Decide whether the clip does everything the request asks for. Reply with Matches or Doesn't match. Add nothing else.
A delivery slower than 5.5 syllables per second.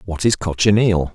Matches